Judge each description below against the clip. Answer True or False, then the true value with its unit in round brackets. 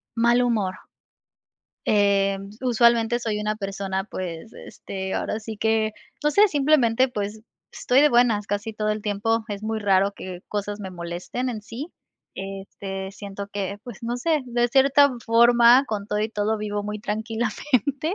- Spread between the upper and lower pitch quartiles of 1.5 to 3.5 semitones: True (3.0 semitones)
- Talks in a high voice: True (215 Hz)